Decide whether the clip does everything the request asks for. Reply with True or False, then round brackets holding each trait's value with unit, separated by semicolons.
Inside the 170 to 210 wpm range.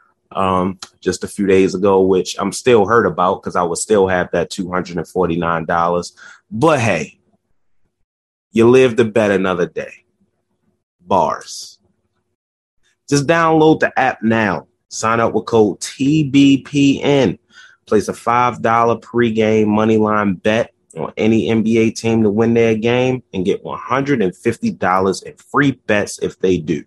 False (135 wpm)